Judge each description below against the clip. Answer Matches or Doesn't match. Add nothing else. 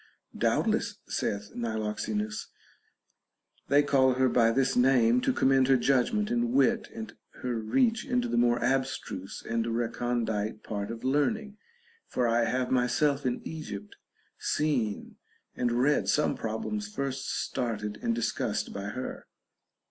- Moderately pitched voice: Doesn't match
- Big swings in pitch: Doesn't match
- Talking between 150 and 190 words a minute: Doesn't match